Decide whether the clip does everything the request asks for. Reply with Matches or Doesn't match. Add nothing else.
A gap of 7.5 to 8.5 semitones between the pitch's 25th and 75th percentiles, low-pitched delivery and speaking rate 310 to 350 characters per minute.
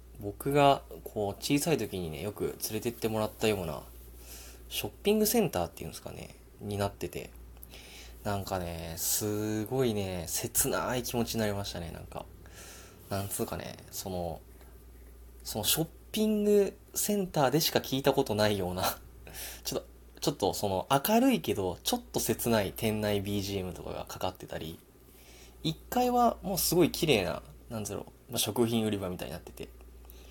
Matches